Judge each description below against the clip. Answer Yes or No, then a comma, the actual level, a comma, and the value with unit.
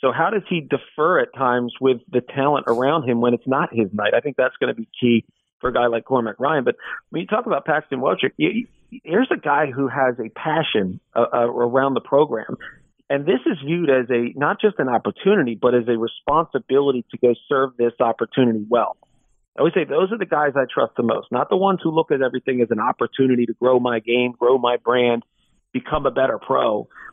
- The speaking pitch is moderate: No, low, 130 Hz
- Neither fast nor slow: No, fast, 225 wpm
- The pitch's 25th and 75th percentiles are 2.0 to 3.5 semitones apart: Yes, narrow, 2.6 semitones